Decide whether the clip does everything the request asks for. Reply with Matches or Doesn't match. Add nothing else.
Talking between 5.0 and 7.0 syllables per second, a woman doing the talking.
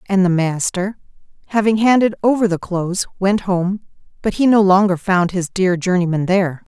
Matches